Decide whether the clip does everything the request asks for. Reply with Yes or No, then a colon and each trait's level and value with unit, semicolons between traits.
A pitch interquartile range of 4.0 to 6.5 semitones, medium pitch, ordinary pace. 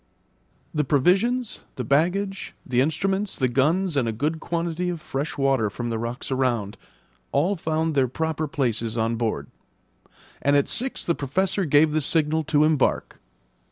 Yes: average, 4.6 semitones; medium, 150 Hz; average, 155 wpm